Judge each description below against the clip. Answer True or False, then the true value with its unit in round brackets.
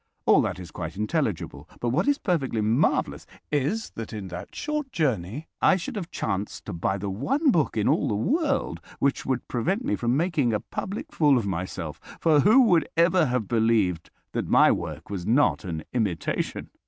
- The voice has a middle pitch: False (125 Hz)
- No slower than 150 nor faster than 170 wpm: False (190 wpm)